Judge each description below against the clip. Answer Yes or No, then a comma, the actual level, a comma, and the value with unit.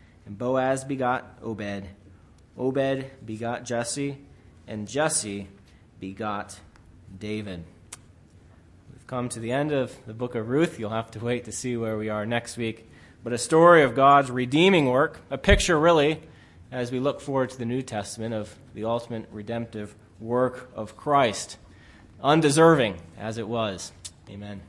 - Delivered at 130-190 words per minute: Yes, average, 150 wpm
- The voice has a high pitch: No, low, 115 Hz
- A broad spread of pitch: No, average, 4.3 semitones